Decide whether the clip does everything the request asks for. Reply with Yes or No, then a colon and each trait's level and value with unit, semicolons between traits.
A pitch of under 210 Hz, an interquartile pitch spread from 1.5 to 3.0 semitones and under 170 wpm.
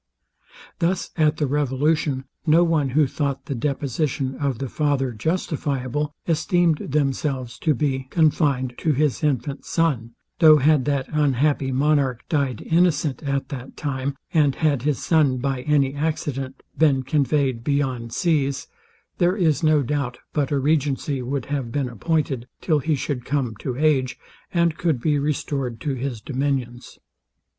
Yes: medium, 140 Hz; average, 2.7 semitones; average, 150 wpm